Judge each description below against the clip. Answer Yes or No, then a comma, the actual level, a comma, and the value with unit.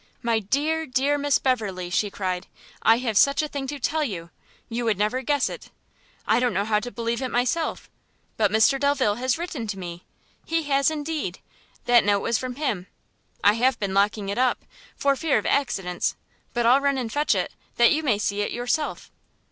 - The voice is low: No, high, 245 Hz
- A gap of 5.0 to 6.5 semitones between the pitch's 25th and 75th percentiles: Yes, average, 5.3 semitones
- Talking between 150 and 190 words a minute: No, average, 200 wpm